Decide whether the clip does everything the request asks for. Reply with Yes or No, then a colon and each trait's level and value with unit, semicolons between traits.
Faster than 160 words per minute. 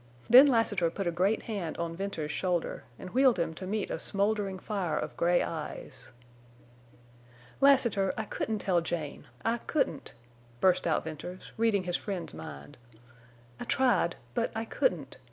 No: average, 155 wpm